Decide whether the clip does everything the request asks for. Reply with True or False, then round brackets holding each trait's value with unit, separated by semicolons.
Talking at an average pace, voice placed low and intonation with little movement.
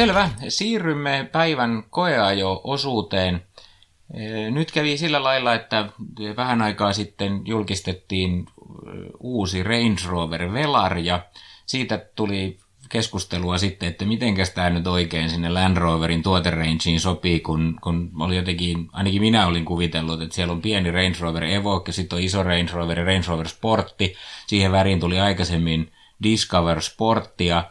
False (135 wpm; 95 Hz; 4.1 semitones)